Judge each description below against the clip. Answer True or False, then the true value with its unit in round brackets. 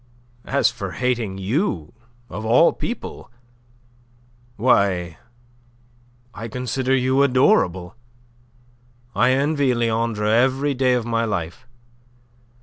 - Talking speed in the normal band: False (95 wpm)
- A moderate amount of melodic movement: True (3.9 semitones)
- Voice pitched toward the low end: True (120 Hz)